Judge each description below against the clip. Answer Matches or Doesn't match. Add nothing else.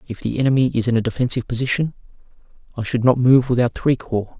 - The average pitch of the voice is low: Matches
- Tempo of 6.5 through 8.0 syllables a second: Matches